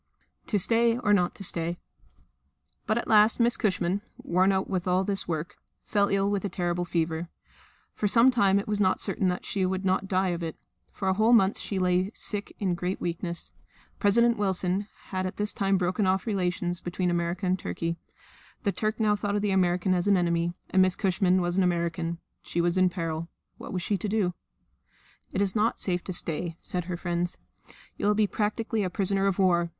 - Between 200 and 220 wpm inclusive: Yes, fast, 205 wpm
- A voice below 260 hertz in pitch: Yes, medium, 185 Hz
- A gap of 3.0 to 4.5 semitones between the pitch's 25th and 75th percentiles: No, narrow, 2.5 semitones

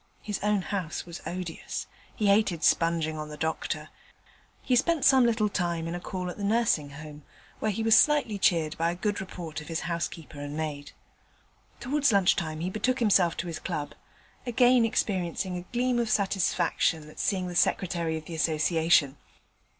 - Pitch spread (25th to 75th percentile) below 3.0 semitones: No, average, 4.8 semitones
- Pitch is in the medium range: Yes, medium, 180 Hz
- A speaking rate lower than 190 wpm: Yes, average, 180 wpm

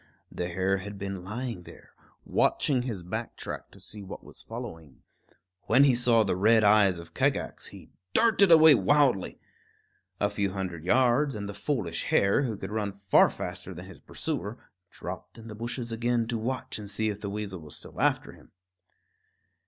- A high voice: No, low, 105 Hz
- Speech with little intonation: No, average, 4.1 semitones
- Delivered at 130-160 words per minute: No, average, 180 wpm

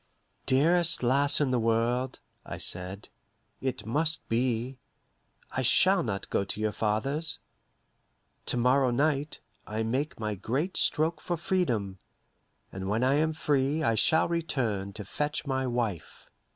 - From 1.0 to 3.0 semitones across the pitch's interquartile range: No, average, 5.1 semitones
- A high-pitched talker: No, low, 130 Hz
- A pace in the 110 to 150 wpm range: Yes, average, 140 wpm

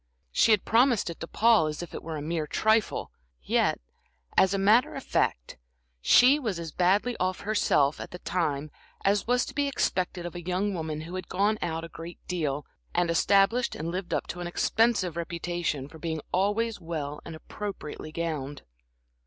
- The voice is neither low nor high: Yes, medium, 175 Hz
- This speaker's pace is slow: No, average, 185 wpm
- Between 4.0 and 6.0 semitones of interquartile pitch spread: Yes, average, 4.4 semitones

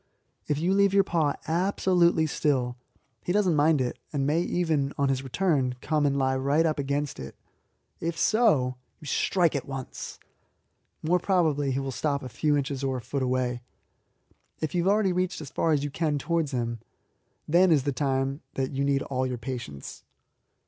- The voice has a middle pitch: Yes, medium, 145 Hz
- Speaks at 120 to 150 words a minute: No, average, 190 wpm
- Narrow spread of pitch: No, average, 4.0 semitones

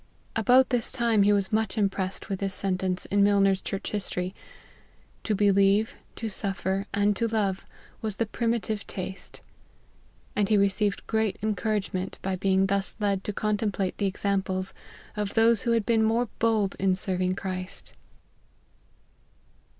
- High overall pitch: Yes, high, 200 Hz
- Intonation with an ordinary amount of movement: No, narrow, 2.2 semitones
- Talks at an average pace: Yes, average, 160 wpm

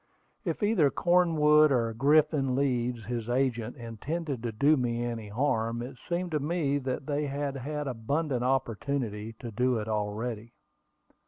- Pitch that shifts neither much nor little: Yes, average, 4.1 semitones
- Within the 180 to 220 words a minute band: No, average, 145 wpm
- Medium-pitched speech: No, low, 130 Hz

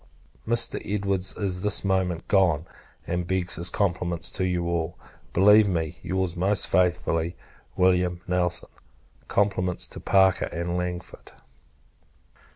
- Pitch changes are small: Yes, narrow, 1.7 semitones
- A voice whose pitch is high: No, very low, 90 Hz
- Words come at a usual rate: No, slow, 120 wpm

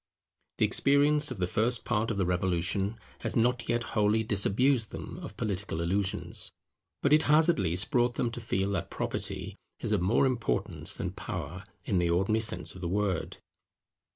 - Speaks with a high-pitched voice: No, low, 105 Hz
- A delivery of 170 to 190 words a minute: Yes, average, 180 wpm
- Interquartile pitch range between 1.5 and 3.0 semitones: No, average, 4.3 semitones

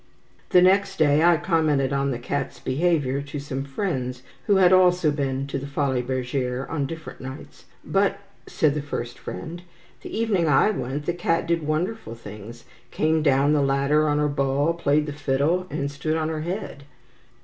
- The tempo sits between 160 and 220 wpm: Yes, average, 180 wpm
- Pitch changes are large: No, average, 3.4 semitones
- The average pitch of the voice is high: No, medium, 145 Hz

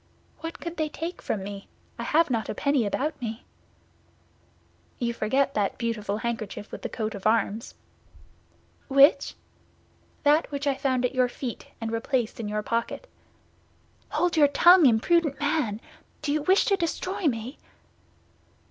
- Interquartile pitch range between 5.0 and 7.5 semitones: Yes, wide, 5.5 semitones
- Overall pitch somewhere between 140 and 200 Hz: No, very high, 260 Hz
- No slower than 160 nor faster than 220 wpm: No, average, 150 wpm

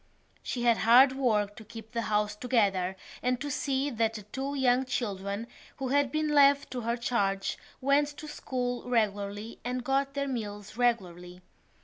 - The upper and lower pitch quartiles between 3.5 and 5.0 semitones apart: Yes, average, 4.2 semitones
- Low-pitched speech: No, high, 240 Hz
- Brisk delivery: No, average, 165 wpm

